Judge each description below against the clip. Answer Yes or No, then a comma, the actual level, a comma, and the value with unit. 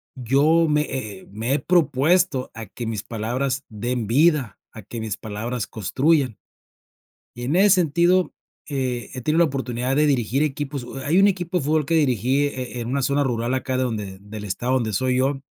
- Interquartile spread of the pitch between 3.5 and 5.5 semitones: Yes, average, 4.2 semitones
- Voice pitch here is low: Yes, low, 130 Hz